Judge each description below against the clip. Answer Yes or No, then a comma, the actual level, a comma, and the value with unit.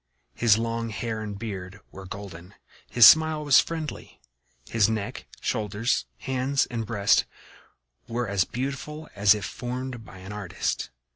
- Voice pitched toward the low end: Yes, low, 110 Hz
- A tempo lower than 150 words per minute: Yes, average, 140 wpm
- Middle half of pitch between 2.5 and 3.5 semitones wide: No, average, 3.9 semitones